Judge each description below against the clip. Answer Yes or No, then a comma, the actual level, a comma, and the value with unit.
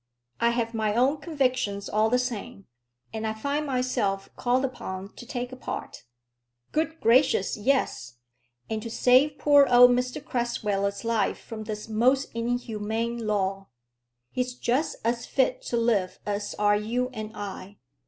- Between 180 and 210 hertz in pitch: No, high, 235 Hz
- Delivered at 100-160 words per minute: Yes, average, 150 wpm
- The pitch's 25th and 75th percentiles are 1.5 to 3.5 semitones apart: Yes, average, 3.2 semitones